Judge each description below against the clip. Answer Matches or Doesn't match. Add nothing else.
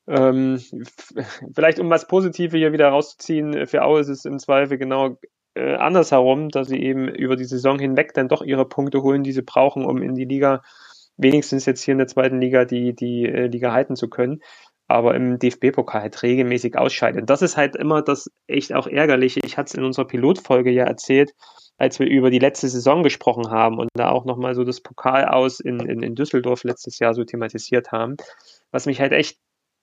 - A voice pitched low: Matches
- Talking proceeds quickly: Matches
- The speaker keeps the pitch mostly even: Matches